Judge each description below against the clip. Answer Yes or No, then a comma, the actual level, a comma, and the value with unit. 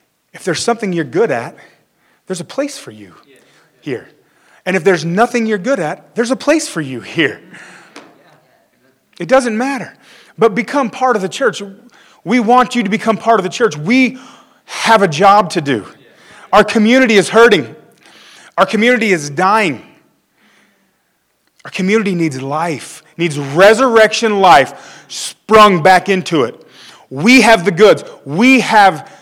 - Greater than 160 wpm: No, average, 150 wpm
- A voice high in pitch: Yes, high, 215 Hz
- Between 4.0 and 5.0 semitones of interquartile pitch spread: Yes, average, 4.5 semitones